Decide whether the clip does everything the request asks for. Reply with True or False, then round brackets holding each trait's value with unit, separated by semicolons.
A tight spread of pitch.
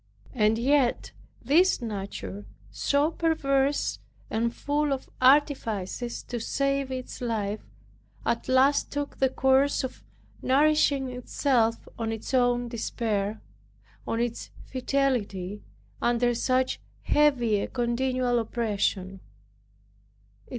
False (3.5 semitones)